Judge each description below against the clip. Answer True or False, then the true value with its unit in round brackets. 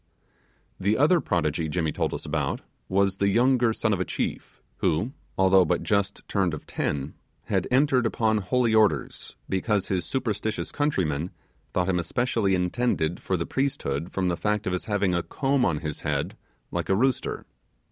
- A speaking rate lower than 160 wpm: False (170 wpm)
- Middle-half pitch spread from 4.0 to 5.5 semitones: True (5.0 semitones)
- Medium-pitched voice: False (100 Hz)